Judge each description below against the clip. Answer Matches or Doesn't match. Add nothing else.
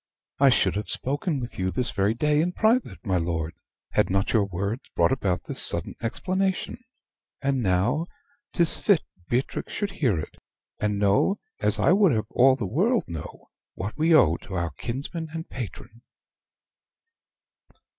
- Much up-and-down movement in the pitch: Matches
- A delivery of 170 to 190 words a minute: Doesn't match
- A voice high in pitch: Doesn't match